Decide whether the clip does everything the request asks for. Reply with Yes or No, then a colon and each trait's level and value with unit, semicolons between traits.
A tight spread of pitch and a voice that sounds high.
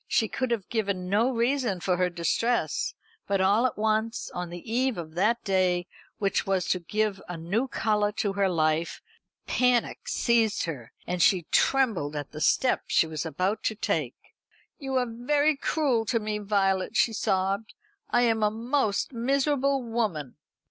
No: average, 4.6 semitones; high, 210 Hz